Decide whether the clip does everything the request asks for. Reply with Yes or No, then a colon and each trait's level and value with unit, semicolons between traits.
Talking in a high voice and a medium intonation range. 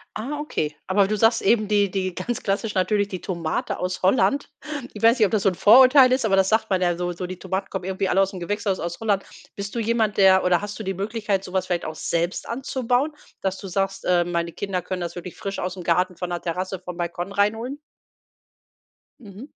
Yes: high, 195 Hz; average, 3.0 semitones